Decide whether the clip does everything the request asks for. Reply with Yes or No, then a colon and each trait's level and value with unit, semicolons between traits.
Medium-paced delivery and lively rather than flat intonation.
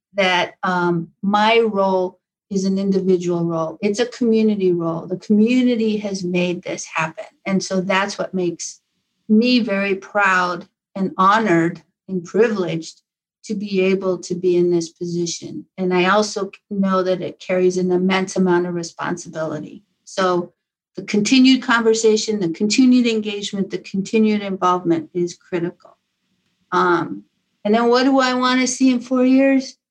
No: average, 145 wpm; average, 3.3 semitones